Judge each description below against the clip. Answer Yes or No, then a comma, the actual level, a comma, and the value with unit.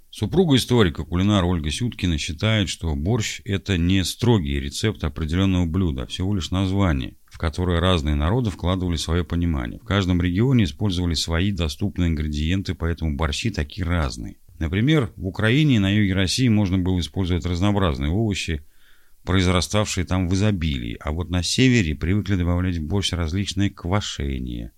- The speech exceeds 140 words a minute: Yes, average, 150 wpm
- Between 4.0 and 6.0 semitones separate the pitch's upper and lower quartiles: No, average, 3.5 semitones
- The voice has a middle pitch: No, very low, 90 Hz